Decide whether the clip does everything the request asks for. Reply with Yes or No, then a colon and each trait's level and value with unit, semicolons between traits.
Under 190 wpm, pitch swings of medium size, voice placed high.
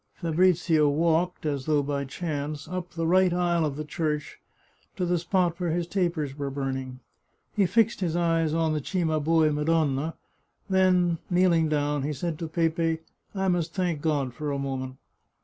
No: average, 170 wpm; average, 3.0 semitones; medium, 160 Hz